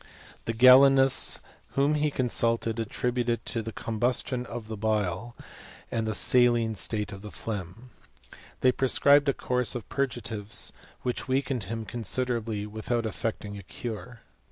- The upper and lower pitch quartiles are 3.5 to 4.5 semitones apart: No, narrow, 2.5 semitones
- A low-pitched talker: Yes, low, 115 Hz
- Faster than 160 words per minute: No, average, 140 wpm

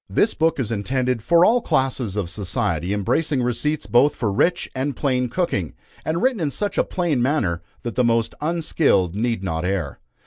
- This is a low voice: Yes, low, 125 Hz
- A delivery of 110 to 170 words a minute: No, average, 180 wpm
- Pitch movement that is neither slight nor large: No, wide, 7.3 semitones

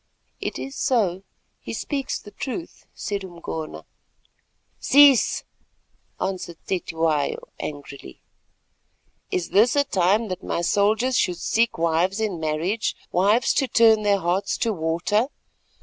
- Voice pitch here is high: Yes, high, 195 Hz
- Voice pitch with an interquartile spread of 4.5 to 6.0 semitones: Yes, average, 5.1 semitones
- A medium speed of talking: No, slow, 120 wpm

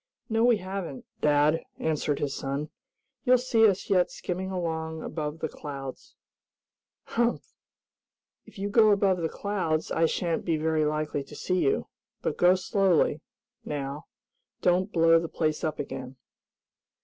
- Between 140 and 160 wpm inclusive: Yes, average, 145 wpm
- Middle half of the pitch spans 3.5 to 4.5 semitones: Yes, average, 4.1 semitones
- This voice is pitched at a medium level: Yes, medium, 165 Hz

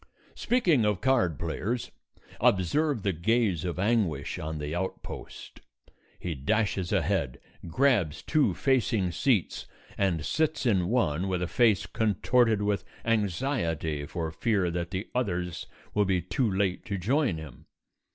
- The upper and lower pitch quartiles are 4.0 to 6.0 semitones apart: Yes, wide, 5.5 semitones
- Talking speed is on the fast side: No, slow, 135 wpm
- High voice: No, very low, 95 Hz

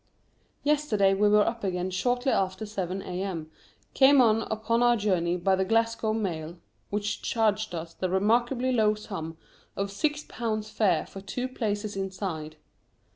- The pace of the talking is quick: No, average, 150 wpm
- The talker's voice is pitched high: Yes, high, 205 Hz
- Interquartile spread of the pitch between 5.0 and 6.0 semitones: No, average, 3.4 semitones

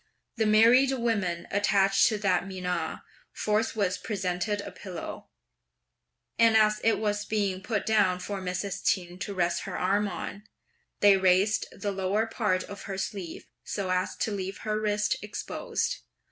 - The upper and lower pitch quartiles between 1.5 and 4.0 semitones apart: Yes, narrow, 2.4 semitones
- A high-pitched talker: Yes, high, 200 Hz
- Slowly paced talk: No, average, 150 wpm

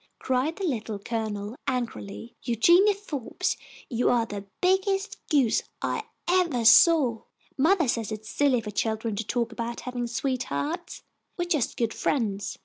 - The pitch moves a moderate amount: No, wide, 6.3 semitones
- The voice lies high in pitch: Yes, high, 245 Hz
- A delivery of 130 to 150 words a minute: Yes, average, 145 wpm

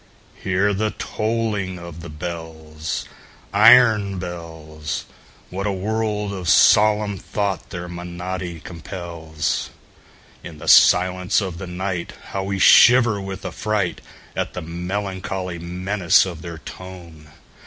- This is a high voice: No, very low, 90 Hz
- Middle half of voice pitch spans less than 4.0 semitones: Yes, average, 2.8 semitones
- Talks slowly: Yes, slow, 100 wpm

